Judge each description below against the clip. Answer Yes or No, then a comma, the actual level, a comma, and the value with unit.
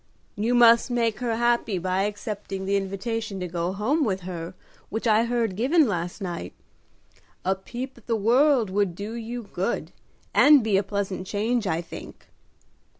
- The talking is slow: No, average, 165 wpm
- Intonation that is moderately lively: Yes, average, 3.7 semitones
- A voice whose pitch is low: No, high, 210 Hz